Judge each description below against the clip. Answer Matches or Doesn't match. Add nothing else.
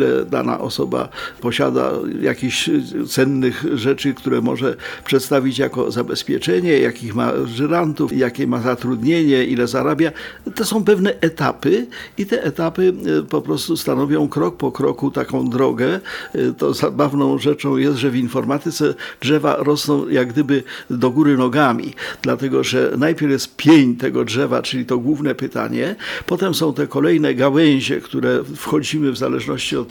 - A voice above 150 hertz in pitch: Doesn't match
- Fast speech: Doesn't match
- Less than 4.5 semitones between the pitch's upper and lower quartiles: Matches